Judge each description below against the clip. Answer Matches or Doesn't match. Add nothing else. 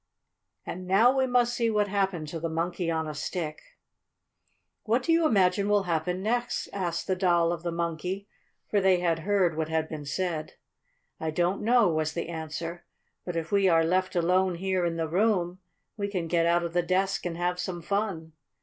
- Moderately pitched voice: Matches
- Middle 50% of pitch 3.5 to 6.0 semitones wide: Doesn't match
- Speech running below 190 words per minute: Doesn't match